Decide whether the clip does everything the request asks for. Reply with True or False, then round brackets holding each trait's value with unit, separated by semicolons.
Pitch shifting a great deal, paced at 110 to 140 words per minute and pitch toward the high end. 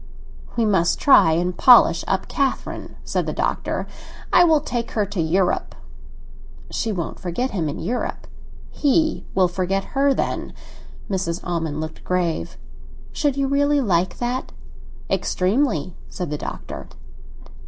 True (7.1 semitones; 135 wpm; 195 Hz)